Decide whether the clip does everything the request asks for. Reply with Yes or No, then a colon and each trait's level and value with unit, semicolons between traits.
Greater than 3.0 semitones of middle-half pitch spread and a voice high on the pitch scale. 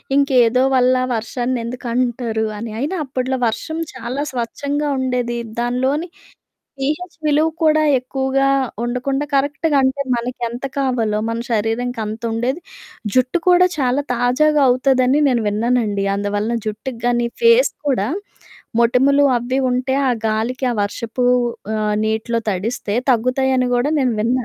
No: average, 2.7 semitones; very high, 250 Hz